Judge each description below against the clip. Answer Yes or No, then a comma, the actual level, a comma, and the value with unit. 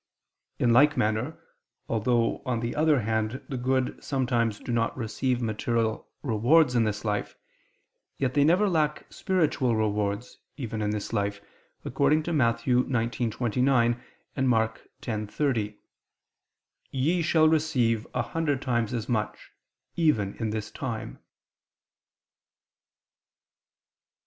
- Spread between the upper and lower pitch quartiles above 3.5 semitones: Yes, average, 3.9 semitones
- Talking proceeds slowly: Yes, slow, 120 wpm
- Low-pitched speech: Yes, low, 120 Hz